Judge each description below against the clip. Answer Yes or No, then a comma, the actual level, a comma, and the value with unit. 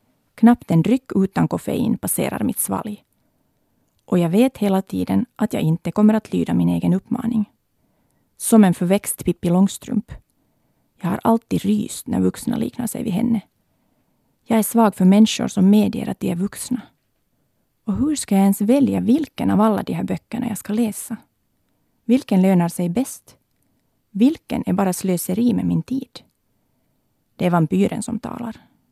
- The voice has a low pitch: No, high, 210 Hz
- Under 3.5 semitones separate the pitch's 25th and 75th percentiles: No, average, 4.1 semitones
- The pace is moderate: Yes, average, 165 wpm